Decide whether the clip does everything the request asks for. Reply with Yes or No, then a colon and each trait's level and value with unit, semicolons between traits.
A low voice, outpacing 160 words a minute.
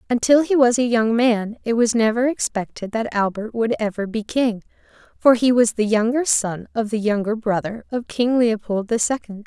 No: high, 225 Hz; average, 195 wpm